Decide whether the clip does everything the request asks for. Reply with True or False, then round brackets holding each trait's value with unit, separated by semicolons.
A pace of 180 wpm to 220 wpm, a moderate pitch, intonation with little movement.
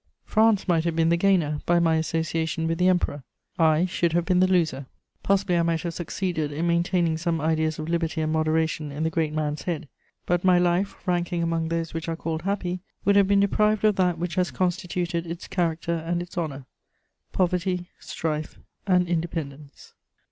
True (190 wpm; 170 Hz; 2.0 semitones)